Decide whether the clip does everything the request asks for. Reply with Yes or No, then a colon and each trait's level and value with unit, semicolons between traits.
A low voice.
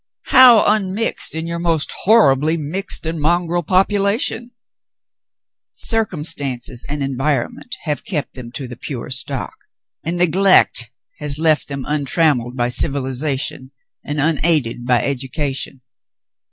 No: medium, 150 Hz